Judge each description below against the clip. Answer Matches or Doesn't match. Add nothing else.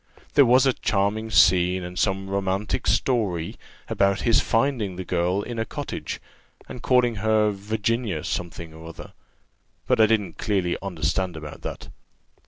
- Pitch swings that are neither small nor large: Matches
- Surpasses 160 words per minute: Doesn't match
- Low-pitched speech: Matches